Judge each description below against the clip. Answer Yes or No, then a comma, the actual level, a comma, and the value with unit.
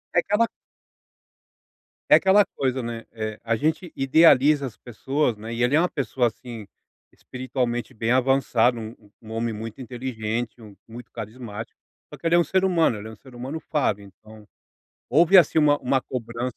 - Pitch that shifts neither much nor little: Yes, average, 4.3 semitones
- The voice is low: Yes, low, 125 Hz